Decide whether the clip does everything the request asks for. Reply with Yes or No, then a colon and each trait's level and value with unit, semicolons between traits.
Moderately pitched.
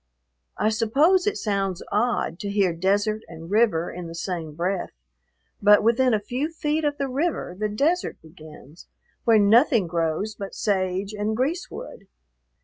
No: high, 210 Hz